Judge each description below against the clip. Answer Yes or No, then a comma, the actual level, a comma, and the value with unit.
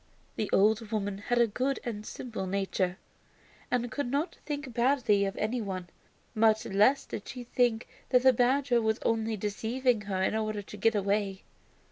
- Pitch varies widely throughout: No, average, 3.4 semitones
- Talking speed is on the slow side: No, average, 170 wpm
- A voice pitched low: No, high, 220 Hz